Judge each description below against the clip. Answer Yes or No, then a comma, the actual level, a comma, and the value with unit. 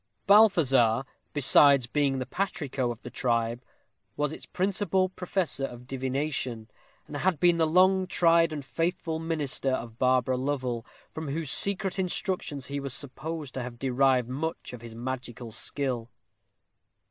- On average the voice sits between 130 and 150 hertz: Yes, medium, 140 Hz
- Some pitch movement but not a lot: Yes, average, 4.7 semitones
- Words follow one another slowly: No, average, 145 wpm